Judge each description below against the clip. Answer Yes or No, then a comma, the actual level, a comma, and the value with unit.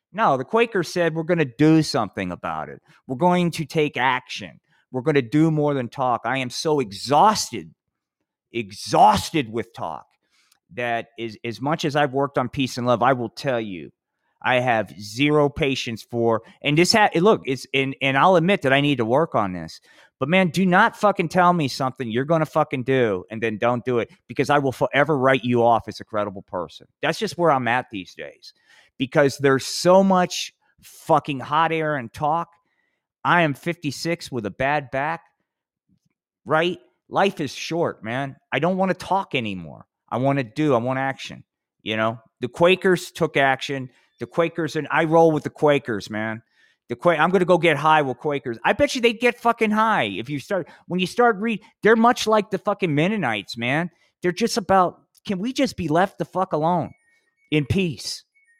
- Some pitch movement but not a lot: No, wide, 5.8 semitones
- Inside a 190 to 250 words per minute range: Yes, average, 200 wpm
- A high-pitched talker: No, medium, 150 Hz